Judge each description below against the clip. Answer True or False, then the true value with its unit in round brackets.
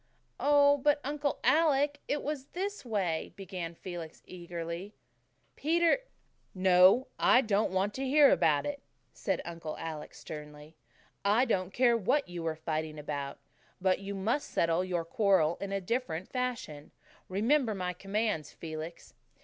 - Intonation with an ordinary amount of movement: False (7.8 semitones)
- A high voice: True (195 Hz)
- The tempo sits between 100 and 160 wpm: True (145 wpm)